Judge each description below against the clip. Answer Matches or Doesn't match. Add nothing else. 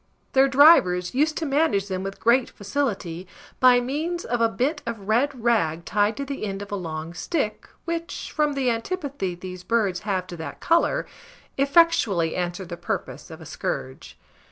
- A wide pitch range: Matches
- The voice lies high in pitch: Matches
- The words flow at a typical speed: Matches